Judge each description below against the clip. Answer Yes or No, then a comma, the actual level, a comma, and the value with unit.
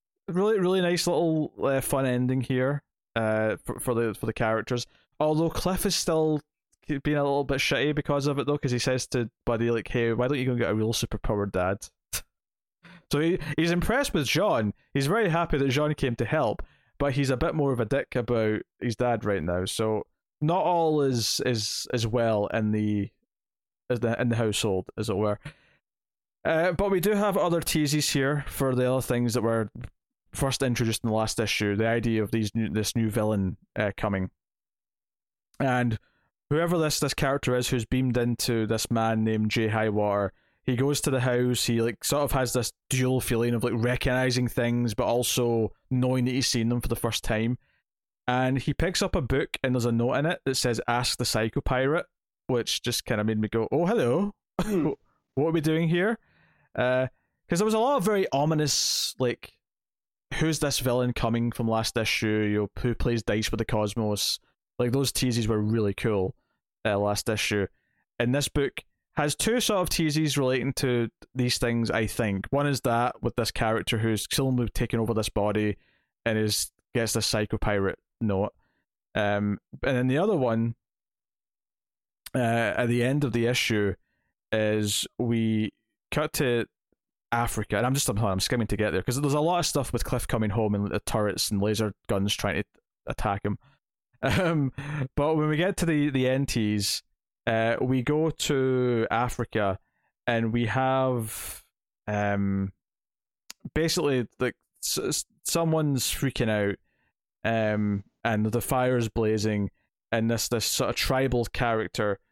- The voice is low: Yes, low, 120 Hz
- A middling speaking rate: Yes, average, 185 wpm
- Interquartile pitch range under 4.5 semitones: Yes, average, 4.0 semitones